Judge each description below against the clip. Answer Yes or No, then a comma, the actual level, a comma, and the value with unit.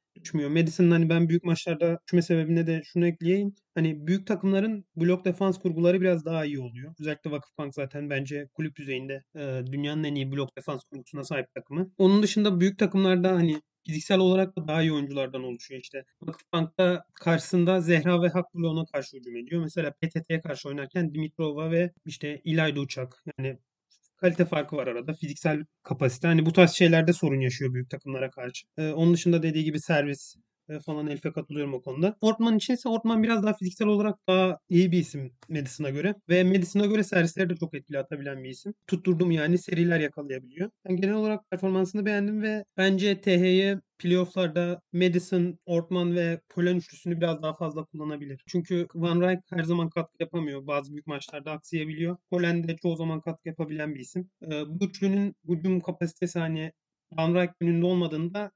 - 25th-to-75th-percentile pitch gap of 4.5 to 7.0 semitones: No, average, 3.3 semitones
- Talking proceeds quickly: Yes, fast, 170 wpm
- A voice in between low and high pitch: Yes, medium, 170 Hz